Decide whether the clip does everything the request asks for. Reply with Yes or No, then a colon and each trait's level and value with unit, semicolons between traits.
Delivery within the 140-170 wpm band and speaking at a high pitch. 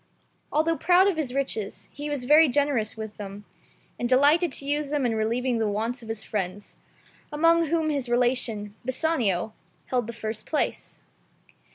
Yes: average, 165 wpm; very high, 250 Hz